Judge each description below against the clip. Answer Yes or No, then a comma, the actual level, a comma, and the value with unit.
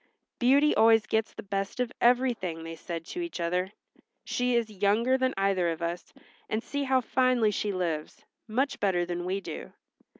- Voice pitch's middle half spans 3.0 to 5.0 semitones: No, wide, 5.6 semitones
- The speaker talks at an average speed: Yes, average, 175 wpm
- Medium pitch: No, high, 210 Hz